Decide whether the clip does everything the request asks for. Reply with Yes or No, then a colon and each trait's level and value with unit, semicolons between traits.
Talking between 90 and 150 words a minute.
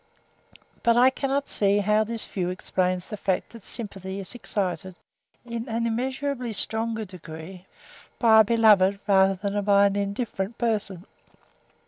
Yes: slow, 135 wpm